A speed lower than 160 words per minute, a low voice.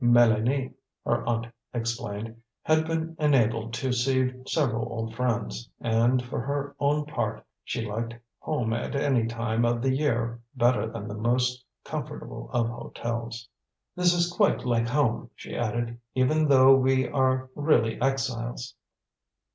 Yes: average, 140 wpm; low, 120 Hz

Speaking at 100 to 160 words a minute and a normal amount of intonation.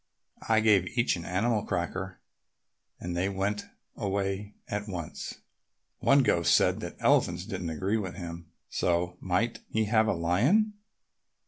Yes: average, 140 wpm; average, 3.6 semitones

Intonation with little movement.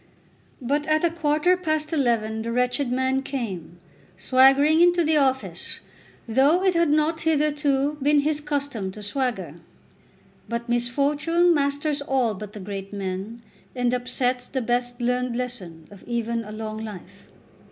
No: average, 4.3 semitones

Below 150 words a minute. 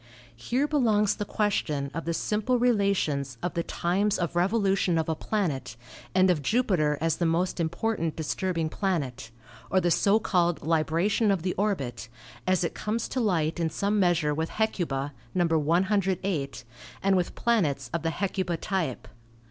No: average, 165 wpm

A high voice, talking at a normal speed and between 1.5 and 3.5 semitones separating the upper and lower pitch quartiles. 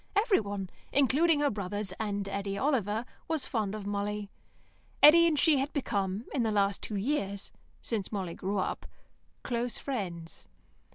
No: high, 210 Hz; average, 150 wpm; wide, 5.5 semitones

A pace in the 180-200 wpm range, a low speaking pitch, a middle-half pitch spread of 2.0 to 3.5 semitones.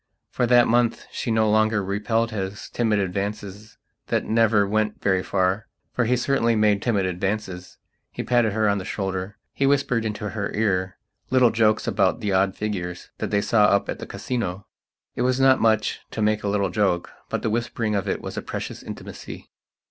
Yes: average, 185 wpm; low, 105 Hz; narrow, 2.5 semitones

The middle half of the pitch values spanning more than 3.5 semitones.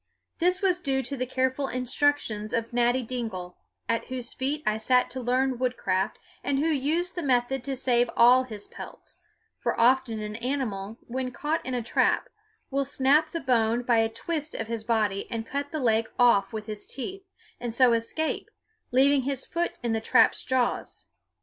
No: average, 3.2 semitones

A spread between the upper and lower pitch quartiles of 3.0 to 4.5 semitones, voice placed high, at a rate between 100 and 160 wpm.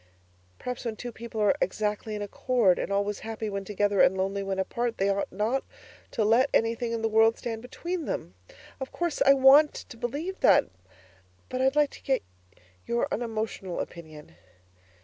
No: average, 3.7 semitones; high, 225 Hz; average, 175 wpm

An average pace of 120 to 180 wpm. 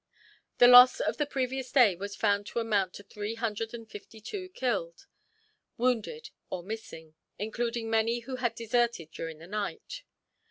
Yes: average, 160 wpm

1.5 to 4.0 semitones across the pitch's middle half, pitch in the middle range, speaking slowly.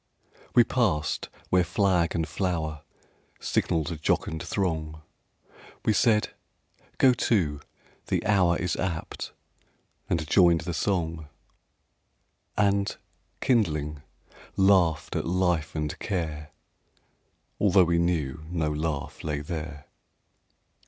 No: average, 3.5 semitones; very low, 85 Hz; slow, 100 wpm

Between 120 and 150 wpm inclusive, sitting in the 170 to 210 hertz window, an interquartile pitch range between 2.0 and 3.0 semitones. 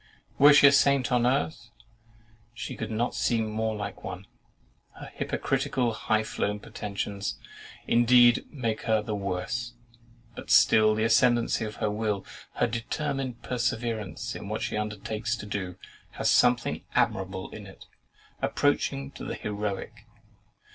No: average, 140 wpm; low, 110 Hz; narrow, 2.5 semitones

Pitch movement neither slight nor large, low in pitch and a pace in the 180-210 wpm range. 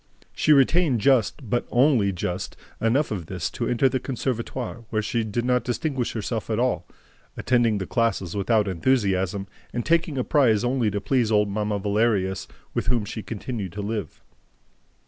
No: average, 3.8 semitones; low, 115 Hz; average, 165 wpm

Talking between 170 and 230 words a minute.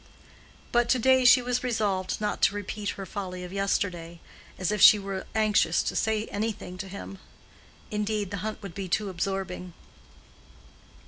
No: average, 160 wpm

